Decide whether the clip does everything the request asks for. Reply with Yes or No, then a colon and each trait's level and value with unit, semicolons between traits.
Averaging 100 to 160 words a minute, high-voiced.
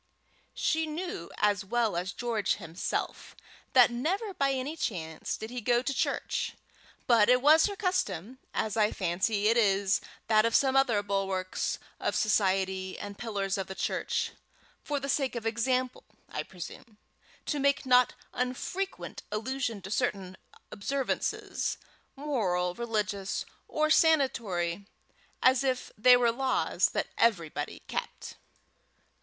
Yes: slow, 135 wpm; high, 230 Hz